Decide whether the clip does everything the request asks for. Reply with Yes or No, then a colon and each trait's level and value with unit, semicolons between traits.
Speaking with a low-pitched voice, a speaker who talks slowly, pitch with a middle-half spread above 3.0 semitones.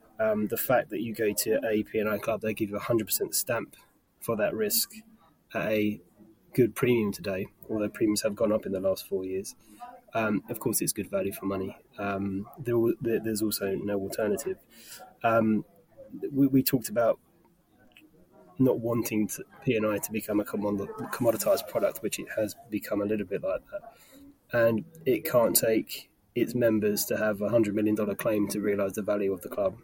No: low, 110 Hz; average, 190 wpm; average, 4.6 semitones